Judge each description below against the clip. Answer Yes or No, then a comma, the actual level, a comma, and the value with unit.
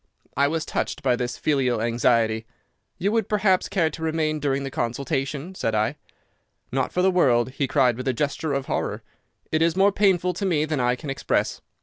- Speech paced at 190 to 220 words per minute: Yes, average, 200 wpm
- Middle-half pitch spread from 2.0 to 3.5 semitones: No, average, 5.3 semitones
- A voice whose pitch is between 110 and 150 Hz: Yes, medium, 140 Hz